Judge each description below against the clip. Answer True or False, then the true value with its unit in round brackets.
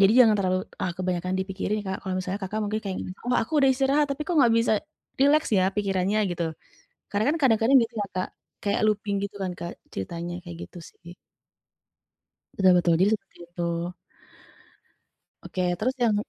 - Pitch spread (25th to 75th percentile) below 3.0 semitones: False (3.6 semitones)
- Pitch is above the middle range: True (200 Hz)